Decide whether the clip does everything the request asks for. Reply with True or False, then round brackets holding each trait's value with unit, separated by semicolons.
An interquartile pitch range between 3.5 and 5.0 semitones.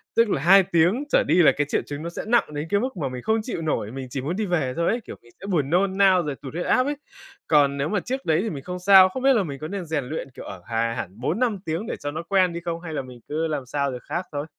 False (5.5 semitones)